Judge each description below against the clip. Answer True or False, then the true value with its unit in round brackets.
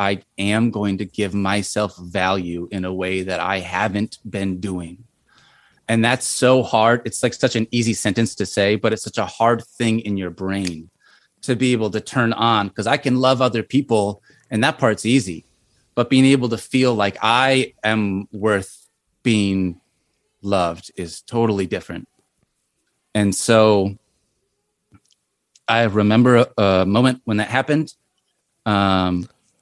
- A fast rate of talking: False (155 wpm)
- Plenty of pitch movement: False (3.6 semitones)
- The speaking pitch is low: True (110 Hz)